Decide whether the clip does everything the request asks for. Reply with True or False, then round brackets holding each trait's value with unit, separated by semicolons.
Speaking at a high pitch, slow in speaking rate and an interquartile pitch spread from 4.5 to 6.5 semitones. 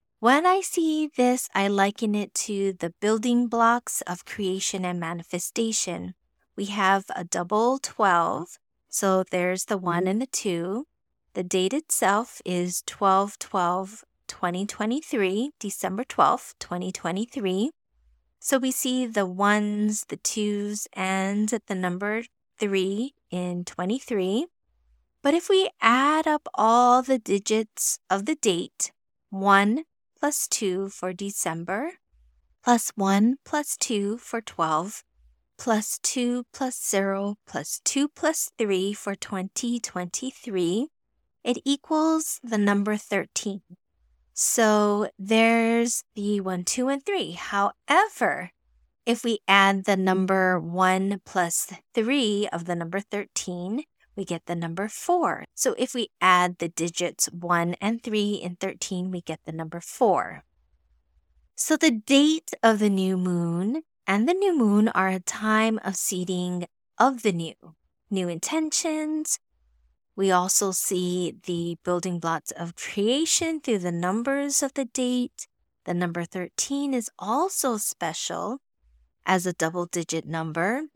True (200 Hz; 130 wpm; 5.2 semitones)